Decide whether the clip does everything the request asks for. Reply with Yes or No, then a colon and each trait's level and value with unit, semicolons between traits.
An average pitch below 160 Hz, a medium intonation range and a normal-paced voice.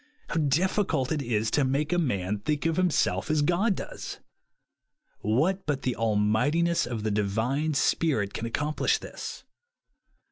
No: medium, 140 Hz; wide, 6.6 semitones; average, 150 wpm